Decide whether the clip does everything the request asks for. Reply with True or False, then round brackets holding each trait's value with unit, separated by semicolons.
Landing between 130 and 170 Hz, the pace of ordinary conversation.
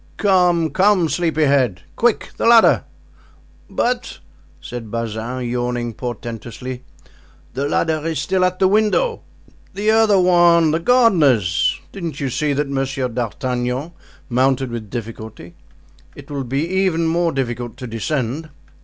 False (140 Hz; 130 wpm)